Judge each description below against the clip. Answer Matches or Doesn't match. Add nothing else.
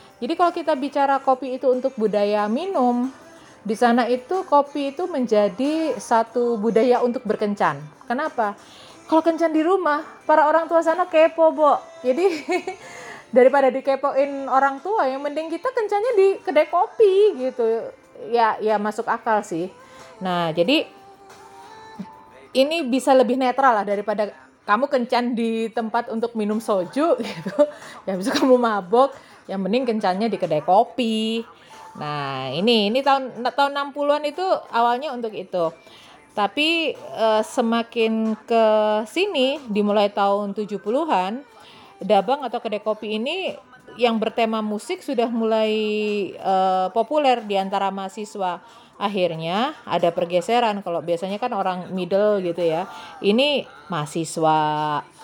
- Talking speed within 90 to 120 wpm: Doesn't match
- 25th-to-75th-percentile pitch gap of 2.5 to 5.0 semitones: Doesn't match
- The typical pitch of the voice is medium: Doesn't match